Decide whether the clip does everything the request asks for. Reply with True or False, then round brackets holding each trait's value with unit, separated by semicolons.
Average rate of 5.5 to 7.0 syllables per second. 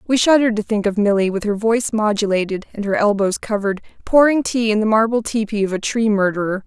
True (6.3 syllables/s)